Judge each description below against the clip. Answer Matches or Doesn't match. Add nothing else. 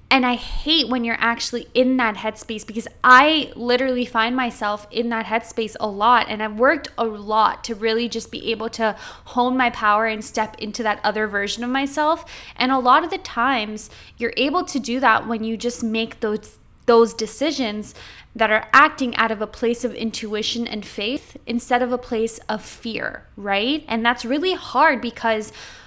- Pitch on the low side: Doesn't match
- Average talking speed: Matches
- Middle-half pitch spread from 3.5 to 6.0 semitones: Doesn't match